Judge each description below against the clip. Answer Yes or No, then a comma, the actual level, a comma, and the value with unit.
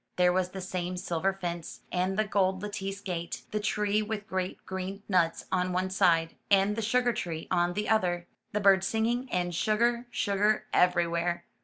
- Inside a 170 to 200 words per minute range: Yes, average, 180 wpm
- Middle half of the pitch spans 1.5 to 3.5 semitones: Yes, average, 2.8 semitones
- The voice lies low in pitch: No, high, 190 Hz